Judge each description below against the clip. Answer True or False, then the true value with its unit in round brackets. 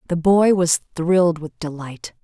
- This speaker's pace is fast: False (160 wpm)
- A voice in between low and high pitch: True (170 Hz)